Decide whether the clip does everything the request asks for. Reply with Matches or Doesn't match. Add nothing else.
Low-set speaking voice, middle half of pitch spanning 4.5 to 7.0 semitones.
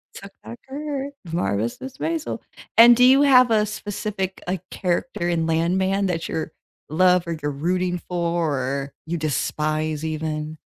Doesn't match